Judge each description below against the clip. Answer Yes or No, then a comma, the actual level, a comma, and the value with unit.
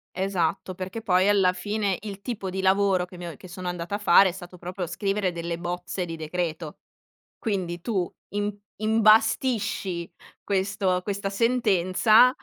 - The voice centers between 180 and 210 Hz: Yes, high, 190 Hz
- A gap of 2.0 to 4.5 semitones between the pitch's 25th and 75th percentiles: Yes, narrow, 2.5 semitones